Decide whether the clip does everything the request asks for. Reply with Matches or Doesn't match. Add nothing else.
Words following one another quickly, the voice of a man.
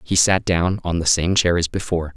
Matches